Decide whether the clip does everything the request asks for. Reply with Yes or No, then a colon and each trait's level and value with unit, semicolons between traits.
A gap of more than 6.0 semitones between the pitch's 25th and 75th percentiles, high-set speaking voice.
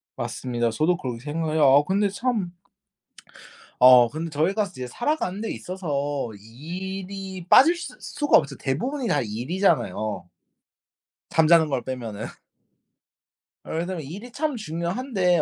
No: wide, 6.6 semitones; medium, 170 Hz